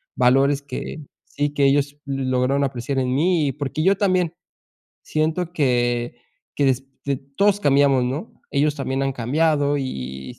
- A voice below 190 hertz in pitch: Yes, medium, 140 Hz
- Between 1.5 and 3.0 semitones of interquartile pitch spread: Yes, average, 2.7 semitones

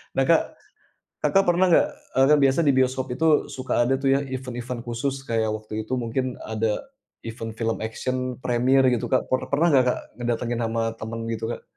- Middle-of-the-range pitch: No, low, 125 Hz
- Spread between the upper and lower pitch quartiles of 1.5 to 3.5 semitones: Yes, narrow, 2.6 semitones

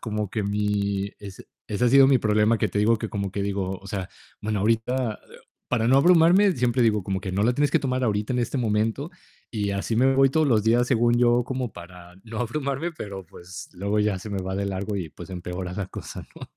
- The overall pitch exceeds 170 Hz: No, low, 105 Hz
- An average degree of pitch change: Yes, average, 3.8 semitones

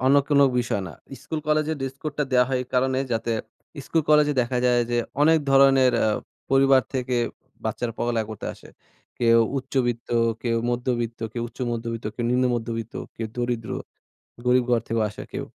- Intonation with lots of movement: No, narrow, 2.4 semitones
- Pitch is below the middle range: Yes, low, 125 Hz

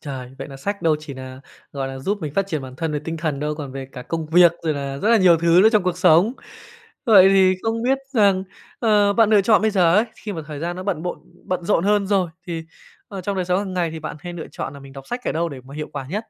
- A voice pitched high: No, medium, 175 Hz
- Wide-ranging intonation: No, average, 5.0 semitones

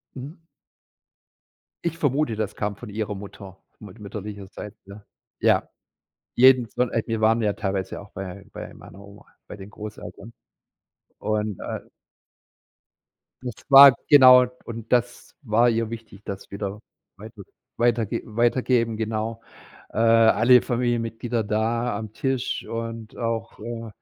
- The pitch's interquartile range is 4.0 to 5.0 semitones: No, narrow, 2.4 semitones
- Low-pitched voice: Yes, low, 115 Hz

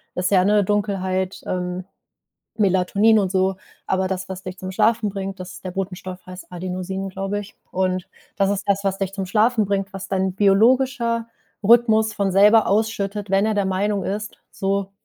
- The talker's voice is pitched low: No, high, 195 Hz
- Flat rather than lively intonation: Yes, narrow, 1.8 semitones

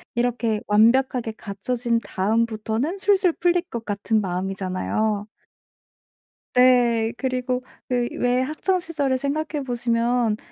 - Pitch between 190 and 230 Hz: No, high, 240 Hz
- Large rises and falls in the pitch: No, average, 3.0 semitones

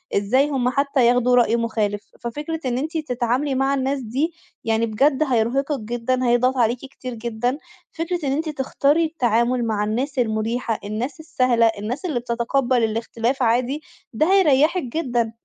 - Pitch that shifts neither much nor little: Yes, average, 3.3 semitones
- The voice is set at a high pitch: Yes, very high, 250 Hz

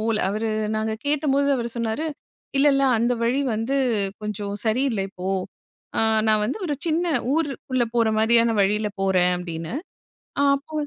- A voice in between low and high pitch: No, high, 225 Hz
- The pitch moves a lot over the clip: No, average, 4.5 semitones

